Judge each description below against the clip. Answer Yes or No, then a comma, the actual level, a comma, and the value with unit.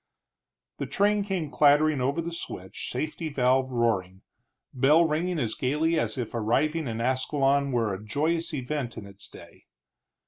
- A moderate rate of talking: Yes, average, 150 wpm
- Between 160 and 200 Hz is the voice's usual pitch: No, medium, 140 Hz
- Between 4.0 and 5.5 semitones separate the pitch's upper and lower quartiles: Yes, average, 4.8 semitones